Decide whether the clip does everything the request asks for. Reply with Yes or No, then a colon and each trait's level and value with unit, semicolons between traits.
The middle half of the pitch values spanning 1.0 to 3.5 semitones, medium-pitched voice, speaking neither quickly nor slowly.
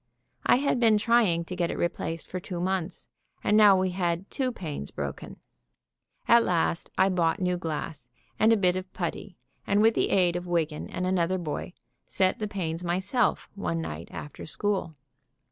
Yes: average, 3.1 semitones; medium, 180 Hz; average, 180 wpm